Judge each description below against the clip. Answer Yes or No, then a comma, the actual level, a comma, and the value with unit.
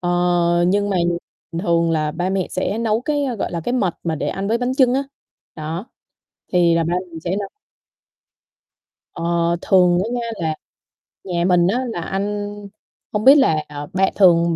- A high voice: No, medium, 180 Hz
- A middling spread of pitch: Yes, average, 3.5 semitones